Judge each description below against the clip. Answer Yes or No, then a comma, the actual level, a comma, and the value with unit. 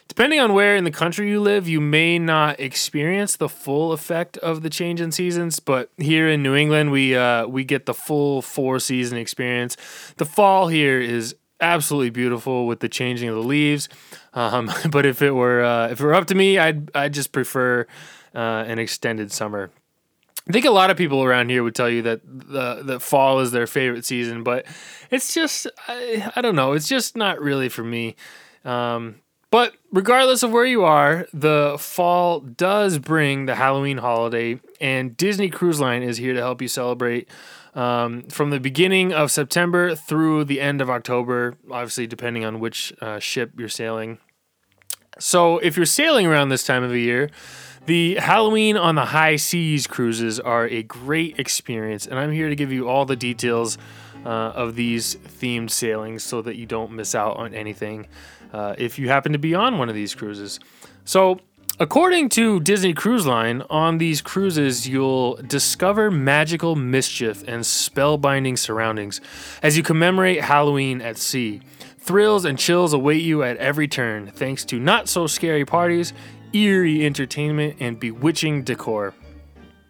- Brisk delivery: No, average, 175 wpm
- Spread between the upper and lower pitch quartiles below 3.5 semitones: No, average, 5.3 semitones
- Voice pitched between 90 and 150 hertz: Yes, low, 135 Hz